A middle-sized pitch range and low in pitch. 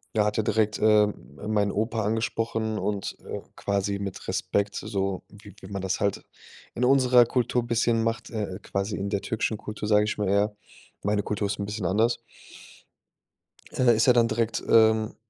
No: narrow, 2.0 semitones; low, 105 Hz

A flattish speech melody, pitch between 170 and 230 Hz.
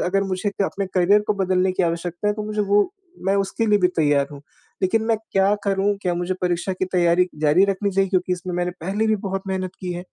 Yes: narrow, 2.0 semitones; high, 190 Hz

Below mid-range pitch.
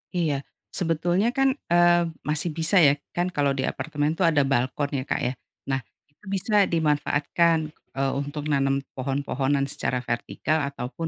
No: medium, 145 Hz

